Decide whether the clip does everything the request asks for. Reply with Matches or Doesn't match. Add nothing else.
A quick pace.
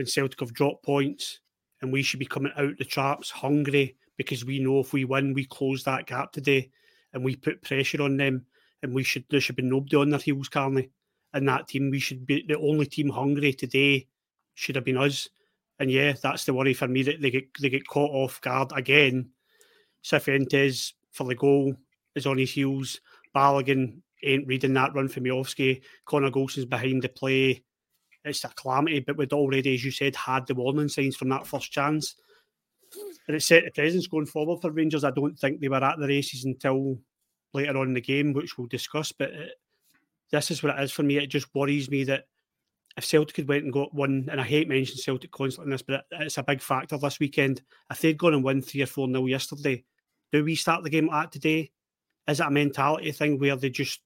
Matches